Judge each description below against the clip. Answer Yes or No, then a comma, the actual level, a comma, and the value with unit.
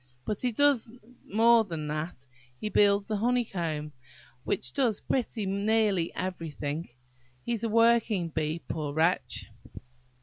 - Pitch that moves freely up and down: Yes, wide, 5.7 semitones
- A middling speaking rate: No, slow, 125 wpm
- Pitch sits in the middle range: No, high, 200 Hz